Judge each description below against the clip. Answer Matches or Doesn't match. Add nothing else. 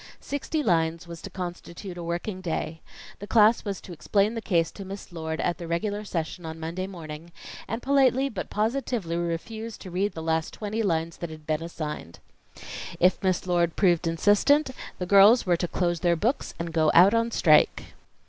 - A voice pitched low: Doesn't match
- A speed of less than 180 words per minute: Doesn't match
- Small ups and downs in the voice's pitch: Doesn't match